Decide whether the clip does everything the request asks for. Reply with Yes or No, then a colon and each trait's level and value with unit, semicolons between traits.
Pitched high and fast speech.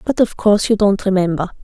Yes: high, 200 Hz; fast, 220 wpm